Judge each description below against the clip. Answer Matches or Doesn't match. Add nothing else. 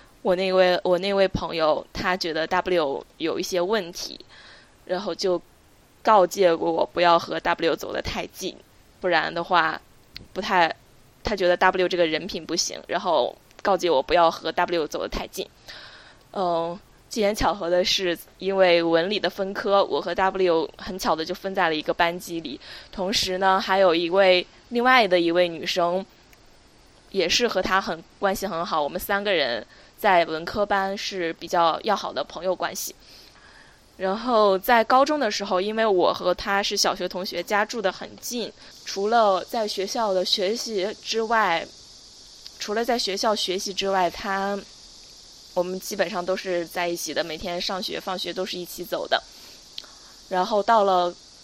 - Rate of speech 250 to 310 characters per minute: Doesn't match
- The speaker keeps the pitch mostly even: Matches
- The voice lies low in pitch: Doesn't match